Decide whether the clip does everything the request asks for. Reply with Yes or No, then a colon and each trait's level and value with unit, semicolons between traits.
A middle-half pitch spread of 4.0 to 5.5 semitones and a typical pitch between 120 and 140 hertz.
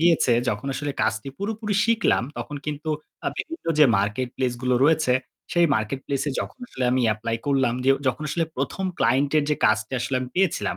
Yes: average, 4.9 semitones; low, 135 Hz